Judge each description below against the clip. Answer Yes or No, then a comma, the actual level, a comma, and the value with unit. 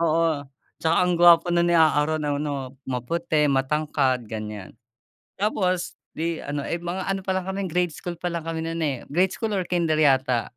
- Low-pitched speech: No, medium, 160 Hz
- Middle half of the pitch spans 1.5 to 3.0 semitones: No, average, 3.6 semitones